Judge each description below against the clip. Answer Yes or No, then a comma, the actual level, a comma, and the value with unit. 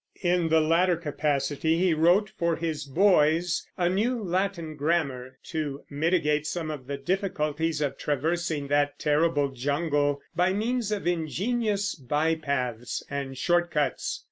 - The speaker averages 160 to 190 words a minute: No, slow, 135 wpm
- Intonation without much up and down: No, average, 3.5 semitones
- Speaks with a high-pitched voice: No, medium, 160 Hz